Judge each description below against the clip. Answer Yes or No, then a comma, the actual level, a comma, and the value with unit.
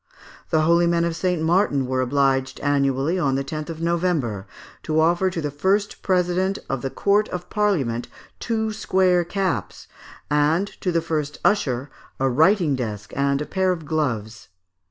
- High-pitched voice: No, medium, 160 Hz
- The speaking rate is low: No, average, 165 wpm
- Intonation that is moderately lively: Yes, average, 5.0 semitones